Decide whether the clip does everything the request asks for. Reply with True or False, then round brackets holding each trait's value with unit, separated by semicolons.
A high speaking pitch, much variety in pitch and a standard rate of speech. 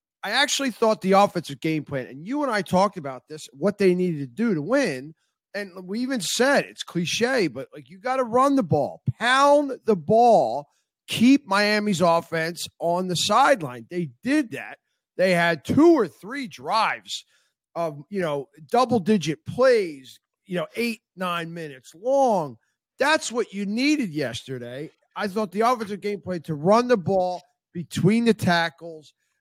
True (195 Hz; 6.6 semitones; 170 wpm)